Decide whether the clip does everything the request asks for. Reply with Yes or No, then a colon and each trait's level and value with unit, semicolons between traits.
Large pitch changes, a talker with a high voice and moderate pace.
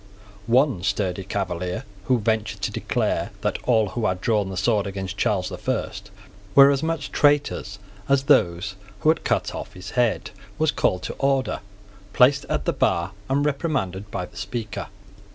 No: wide, 6.1 semitones; low, 110 Hz; average, 170 wpm